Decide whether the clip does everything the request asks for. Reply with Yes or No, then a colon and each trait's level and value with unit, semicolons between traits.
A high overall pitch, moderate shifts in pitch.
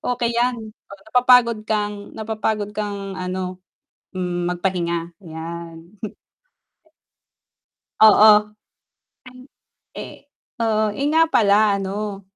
Yes: high, 205 Hz; average, 3.1 semitones